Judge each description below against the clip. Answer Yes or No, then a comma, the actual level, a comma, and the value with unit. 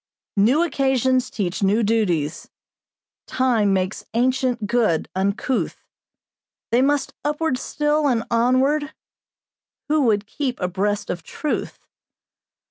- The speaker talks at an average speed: No, slow, 105 wpm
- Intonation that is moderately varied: Yes, average, 4.9 semitones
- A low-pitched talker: No, high, 240 Hz